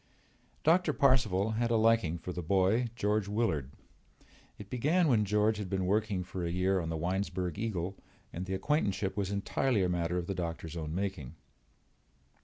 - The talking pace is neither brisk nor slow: Yes, average, 175 wpm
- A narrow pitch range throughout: No, average, 3.7 semitones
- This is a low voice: Yes, very low, 95 Hz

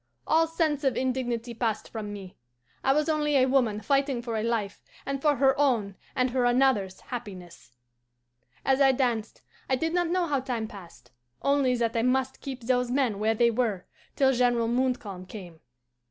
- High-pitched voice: Yes, very high, 250 Hz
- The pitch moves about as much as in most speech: Yes, average, 3.5 semitones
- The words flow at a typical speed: Yes, average, 180 wpm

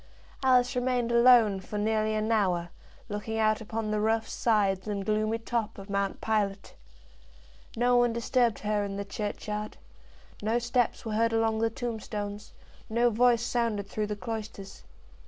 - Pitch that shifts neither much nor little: No, narrow, 2.0 semitones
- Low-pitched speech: No, high, 220 Hz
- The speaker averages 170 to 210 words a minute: No, average, 155 wpm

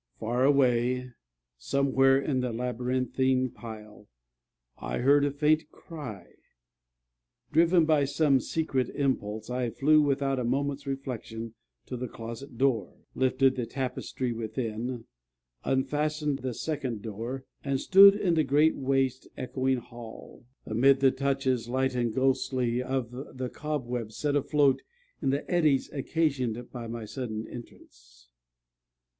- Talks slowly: Yes, slow, 125 wpm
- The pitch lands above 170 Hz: No, low, 130 Hz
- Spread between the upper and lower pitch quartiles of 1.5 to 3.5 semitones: Yes, narrow, 2.6 semitones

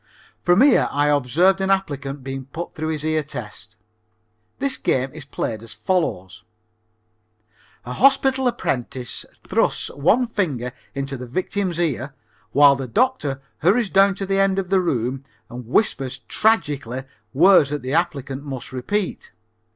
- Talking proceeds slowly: No, average, 145 wpm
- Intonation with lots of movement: Yes, wide, 6.6 semitones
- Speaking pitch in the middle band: Yes, medium, 145 Hz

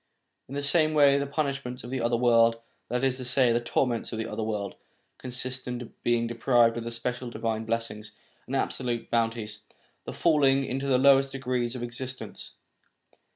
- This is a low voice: Yes, low, 125 Hz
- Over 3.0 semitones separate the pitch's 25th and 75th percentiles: No, narrow, 2.5 semitones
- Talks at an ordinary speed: Yes, average, 190 wpm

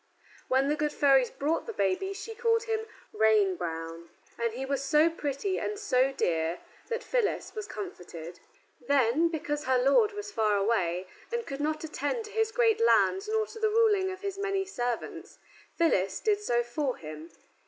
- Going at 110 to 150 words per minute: No, average, 175 wpm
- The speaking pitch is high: Yes, very high, 295 Hz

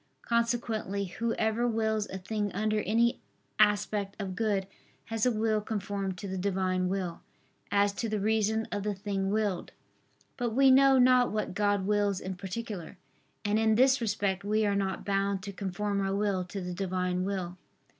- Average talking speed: Yes, average, 170 wpm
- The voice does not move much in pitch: Yes, narrow, 2.2 semitones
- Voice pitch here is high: Yes, high, 205 Hz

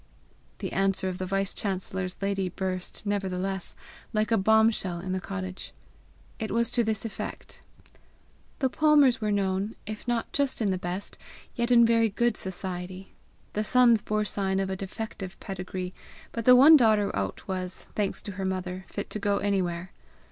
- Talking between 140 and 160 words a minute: No, average, 170 wpm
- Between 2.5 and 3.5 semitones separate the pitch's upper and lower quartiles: Yes, average, 2.8 semitones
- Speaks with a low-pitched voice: No, high, 195 Hz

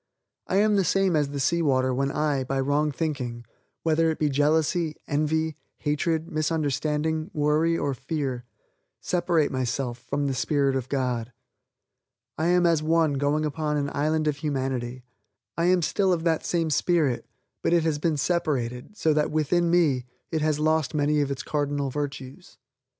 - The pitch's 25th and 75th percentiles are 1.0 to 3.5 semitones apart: Yes, average, 2.7 semitones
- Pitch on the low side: No, medium, 150 Hz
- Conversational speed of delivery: Yes, average, 165 wpm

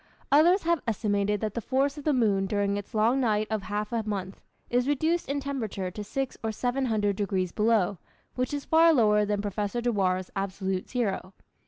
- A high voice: Yes, high, 215 Hz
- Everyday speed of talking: Yes, average, 190 wpm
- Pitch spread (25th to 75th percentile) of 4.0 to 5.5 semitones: Yes, average, 4.5 semitones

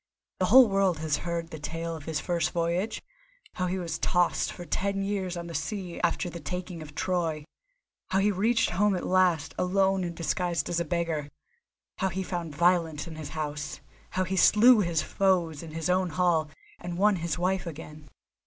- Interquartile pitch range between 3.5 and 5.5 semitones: No, narrow, 2.5 semitones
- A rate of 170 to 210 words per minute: Yes, average, 190 wpm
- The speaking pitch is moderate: Yes, medium, 175 Hz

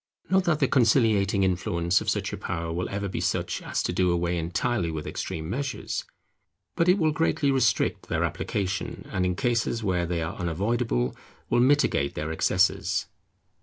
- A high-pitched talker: No, very low, 95 Hz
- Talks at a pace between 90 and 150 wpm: No, average, 170 wpm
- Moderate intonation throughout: No, wide, 5.9 semitones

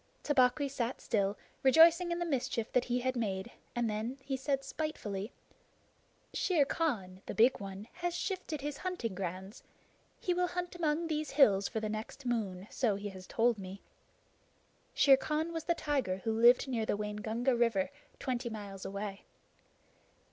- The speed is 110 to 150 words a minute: No, average, 160 wpm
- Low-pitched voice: No, high, 240 Hz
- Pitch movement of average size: No, wide, 6.1 semitones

